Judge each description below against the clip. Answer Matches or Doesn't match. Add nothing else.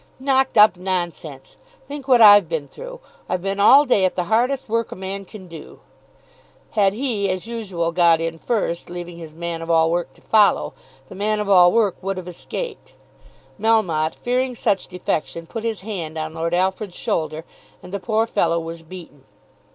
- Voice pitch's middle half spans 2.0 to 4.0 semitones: Doesn't match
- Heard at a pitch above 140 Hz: Matches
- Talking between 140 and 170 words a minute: Doesn't match